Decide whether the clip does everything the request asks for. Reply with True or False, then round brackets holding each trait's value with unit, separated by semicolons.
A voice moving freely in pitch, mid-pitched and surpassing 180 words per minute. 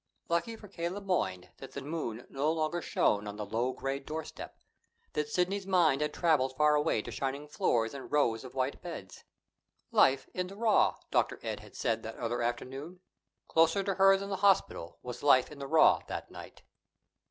True (5.8 semitones; 150 Hz; 190 wpm)